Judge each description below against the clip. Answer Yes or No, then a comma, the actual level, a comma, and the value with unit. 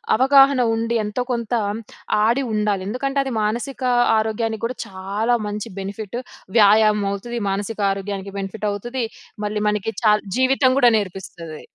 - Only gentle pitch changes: No, average, 3.0 semitones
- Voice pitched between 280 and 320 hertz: No, high, 215 Hz